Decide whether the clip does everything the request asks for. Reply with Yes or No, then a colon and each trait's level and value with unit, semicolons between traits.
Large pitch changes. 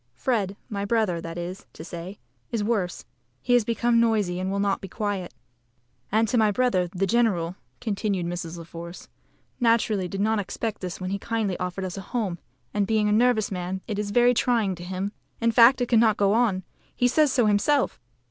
No: average, 3.8 semitones